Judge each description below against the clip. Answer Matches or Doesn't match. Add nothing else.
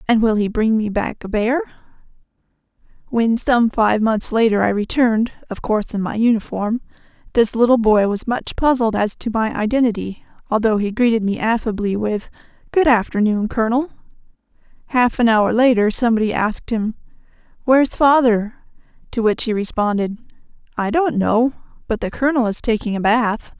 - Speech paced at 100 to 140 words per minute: Doesn't match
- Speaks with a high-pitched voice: Matches